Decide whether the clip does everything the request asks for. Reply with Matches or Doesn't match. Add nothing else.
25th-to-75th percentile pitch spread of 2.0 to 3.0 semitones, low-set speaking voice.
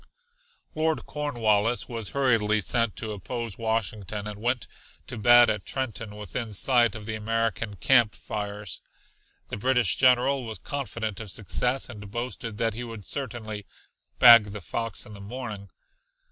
Matches